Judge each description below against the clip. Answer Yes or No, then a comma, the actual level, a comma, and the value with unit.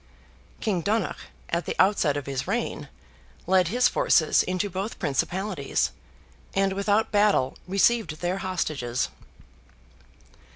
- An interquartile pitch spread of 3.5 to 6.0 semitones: Yes, average, 4.6 semitones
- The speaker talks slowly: Yes, slow, 115 wpm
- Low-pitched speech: No, medium, 185 Hz